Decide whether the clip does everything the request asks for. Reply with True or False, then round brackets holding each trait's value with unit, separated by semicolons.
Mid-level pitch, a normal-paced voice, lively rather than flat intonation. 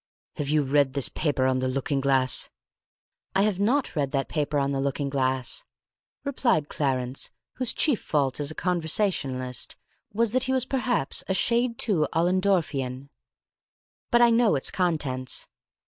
True (150 Hz; 155 wpm; 7.4 semitones)